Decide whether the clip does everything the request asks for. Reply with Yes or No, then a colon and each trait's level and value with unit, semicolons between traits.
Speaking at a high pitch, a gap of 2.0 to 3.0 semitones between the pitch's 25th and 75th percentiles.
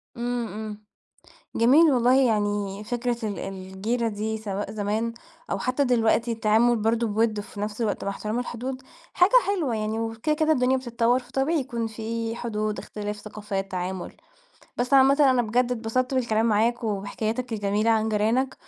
Yes: high, 225 Hz; average, 2.7 semitones